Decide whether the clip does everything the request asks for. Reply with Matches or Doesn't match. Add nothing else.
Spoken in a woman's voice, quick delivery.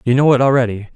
Doesn't match